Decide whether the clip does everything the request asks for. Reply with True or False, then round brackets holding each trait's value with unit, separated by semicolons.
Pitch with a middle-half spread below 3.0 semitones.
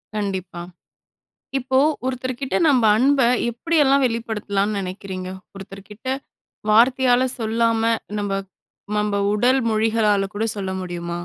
False (4.2 semitones)